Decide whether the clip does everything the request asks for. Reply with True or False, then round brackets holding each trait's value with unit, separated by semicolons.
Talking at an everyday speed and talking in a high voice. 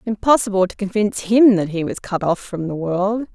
False (215 wpm; 200 Hz)